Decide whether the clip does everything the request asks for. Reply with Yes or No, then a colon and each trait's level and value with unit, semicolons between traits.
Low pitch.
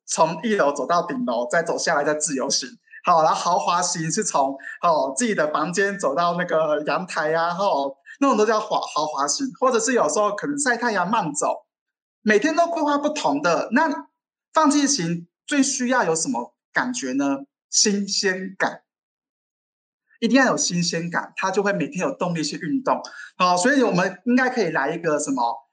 No: high, 190 Hz